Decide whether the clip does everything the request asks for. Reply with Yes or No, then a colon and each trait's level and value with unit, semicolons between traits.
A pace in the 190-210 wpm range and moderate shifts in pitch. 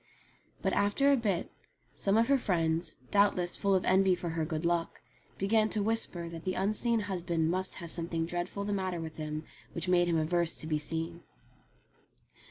No: average, 180 wpm; average, 3.3 semitones